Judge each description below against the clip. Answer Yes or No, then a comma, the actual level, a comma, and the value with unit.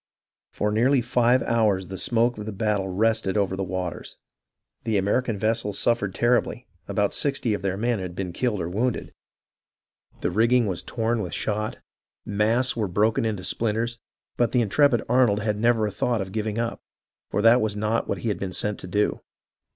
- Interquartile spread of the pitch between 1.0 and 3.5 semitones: Yes, average, 2.8 semitones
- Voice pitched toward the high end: No, low, 110 Hz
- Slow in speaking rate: No, average, 180 wpm